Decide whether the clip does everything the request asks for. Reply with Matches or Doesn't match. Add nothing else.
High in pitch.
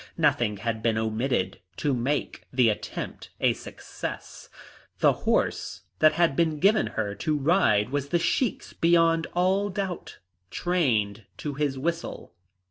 Doesn't match